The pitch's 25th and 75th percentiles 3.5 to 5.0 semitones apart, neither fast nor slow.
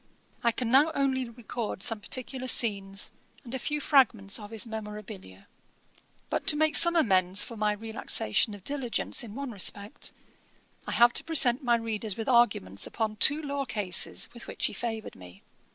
Yes: average, 4.0 semitones; average, 170 wpm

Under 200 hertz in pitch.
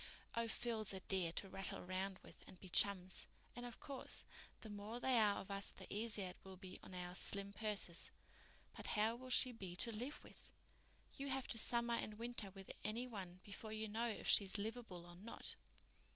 No: high, 210 Hz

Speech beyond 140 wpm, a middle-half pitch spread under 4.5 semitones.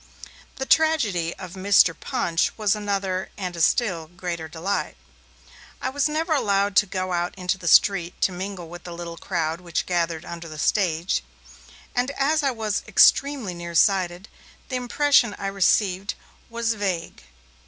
Yes: average, 155 wpm; average, 4.1 semitones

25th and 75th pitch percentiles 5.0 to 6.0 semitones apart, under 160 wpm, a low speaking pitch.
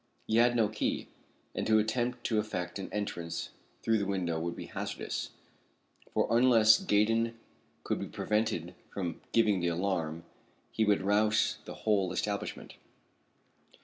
No: average, 3.7 semitones; average, 145 wpm; low, 105 Hz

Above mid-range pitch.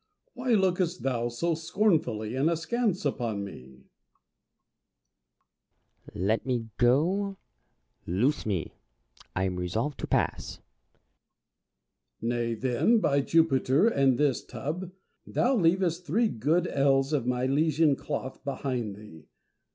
No: medium, 140 Hz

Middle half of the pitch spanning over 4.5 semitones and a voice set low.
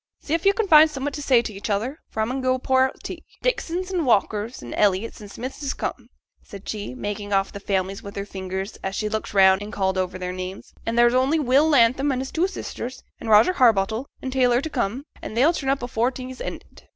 No: average, 5.1 semitones; high, 240 Hz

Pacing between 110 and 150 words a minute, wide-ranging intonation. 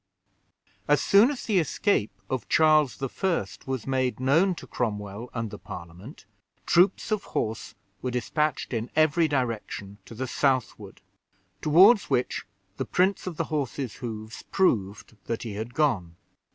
Yes: average, 145 wpm; wide, 6.1 semitones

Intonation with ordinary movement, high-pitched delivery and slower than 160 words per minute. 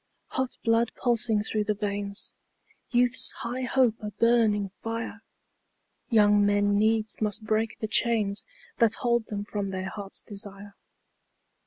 No: narrow, 2.1 semitones; high, 215 Hz; slow, 135 wpm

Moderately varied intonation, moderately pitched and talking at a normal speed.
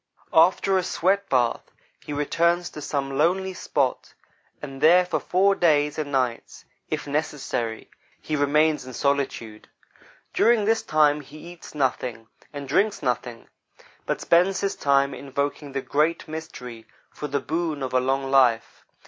Yes: average, 3.9 semitones; medium, 145 Hz; average, 145 wpm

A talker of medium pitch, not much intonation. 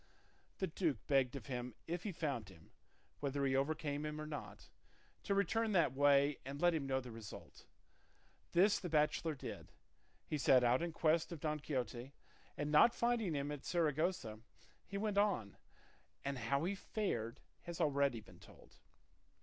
No: medium, 145 Hz; average, 4.4 semitones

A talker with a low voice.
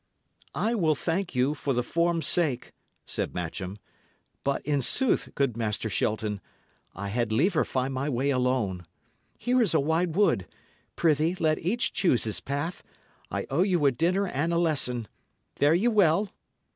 No: medium, 145 Hz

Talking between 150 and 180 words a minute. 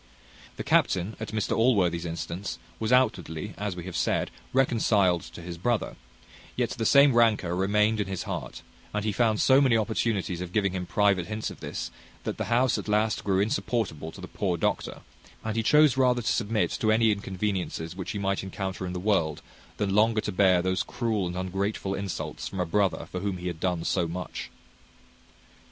No: average, 195 wpm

